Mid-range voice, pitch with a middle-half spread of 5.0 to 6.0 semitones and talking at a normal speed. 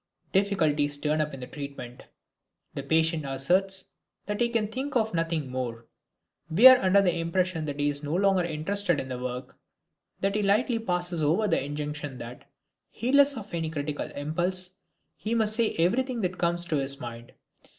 Yes: medium, 170 Hz; wide, 5.5 semitones; average, 175 wpm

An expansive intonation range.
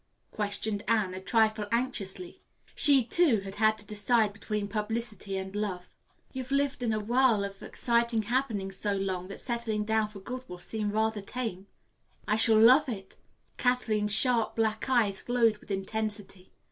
No: average, 2.7 semitones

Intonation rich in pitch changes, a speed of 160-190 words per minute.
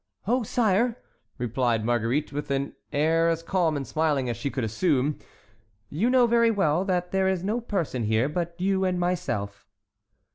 Yes: wide, 5.9 semitones; average, 170 wpm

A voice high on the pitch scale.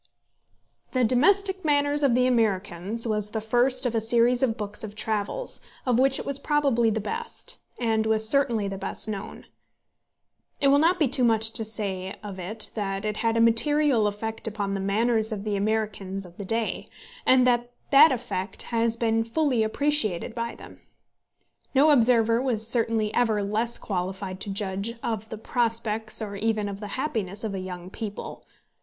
Yes: high, 225 Hz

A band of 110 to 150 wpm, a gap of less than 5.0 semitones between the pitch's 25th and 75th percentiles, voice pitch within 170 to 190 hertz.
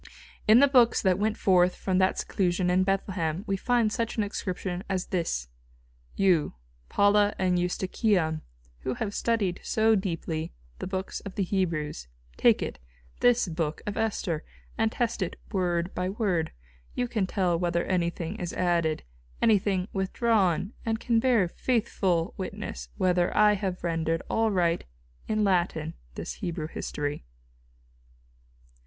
Yes: average, 140 wpm; average, 3.4 semitones; medium, 185 Hz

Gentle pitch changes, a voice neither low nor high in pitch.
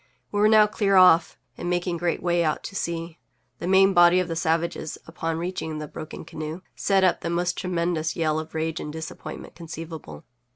Yes: narrow, 2.1 semitones; medium, 170 Hz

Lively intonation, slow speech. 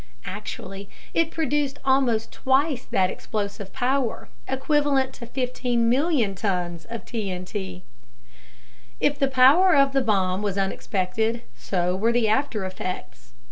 Yes: wide, 5.7 semitones; slow, 125 wpm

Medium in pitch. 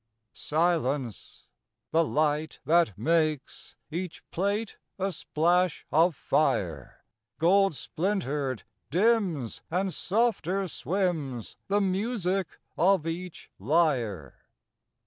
Yes: medium, 170 Hz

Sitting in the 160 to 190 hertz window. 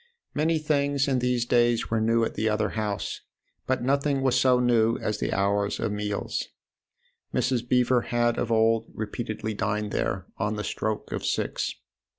No: low, 115 Hz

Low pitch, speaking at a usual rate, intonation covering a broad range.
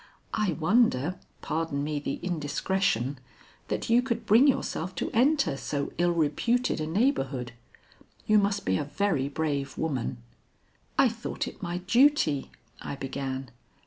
No: medium, 160 Hz; average, 145 wpm; wide, 6.9 semitones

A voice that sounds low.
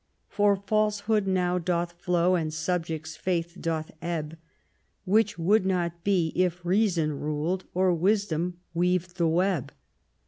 No: medium, 180 Hz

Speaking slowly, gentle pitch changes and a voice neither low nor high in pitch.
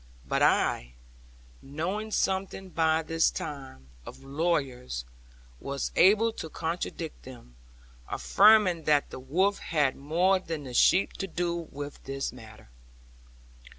No: slow, 120 wpm; average, 5.2 semitones; medium, 160 Hz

